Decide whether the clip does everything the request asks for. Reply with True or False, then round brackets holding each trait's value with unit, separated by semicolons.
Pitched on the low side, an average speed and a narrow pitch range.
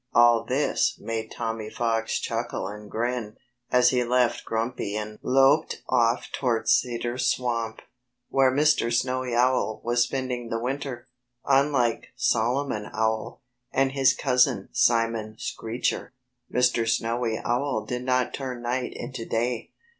False (120 Hz; 130 wpm; 2.0 semitones)